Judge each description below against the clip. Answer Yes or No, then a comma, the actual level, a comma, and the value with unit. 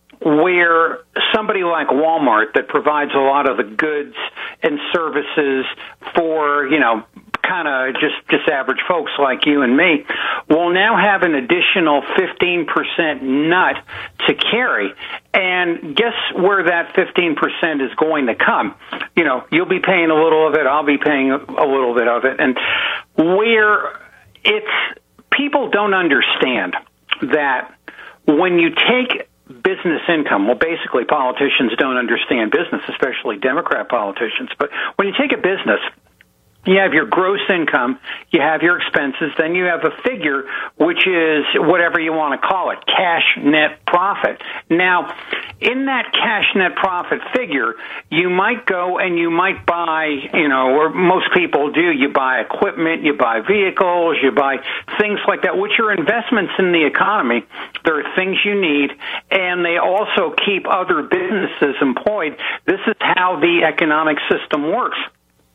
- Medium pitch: Yes, medium, 170 Hz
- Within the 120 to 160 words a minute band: Yes, average, 155 wpm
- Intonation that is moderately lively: Yes, average, 4.2 semitones